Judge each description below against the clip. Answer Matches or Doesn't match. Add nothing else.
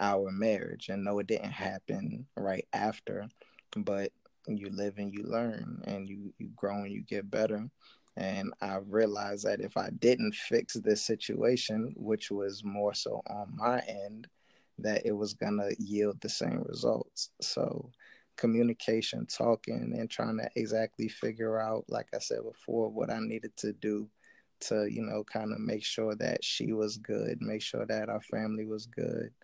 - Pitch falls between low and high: Doesn't match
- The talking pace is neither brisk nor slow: Matches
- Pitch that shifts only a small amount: Matches